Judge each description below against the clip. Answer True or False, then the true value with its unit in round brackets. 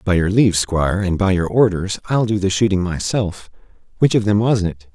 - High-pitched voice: False (100 Hz)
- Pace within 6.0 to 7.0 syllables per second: False (5.4 syllables/s)